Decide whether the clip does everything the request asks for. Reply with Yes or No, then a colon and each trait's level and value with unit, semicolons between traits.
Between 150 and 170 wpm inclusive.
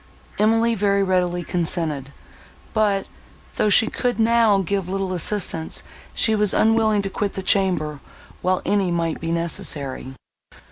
No: slow, 135 wpm